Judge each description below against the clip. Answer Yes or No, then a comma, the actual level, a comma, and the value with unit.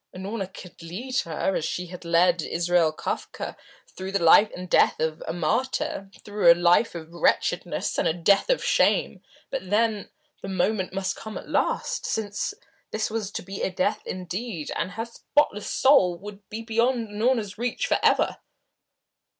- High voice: Yes, high, 195 Hz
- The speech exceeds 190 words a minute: No, average, 165 wpm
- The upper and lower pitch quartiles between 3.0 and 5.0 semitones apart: Yes, average, 4.0 semitones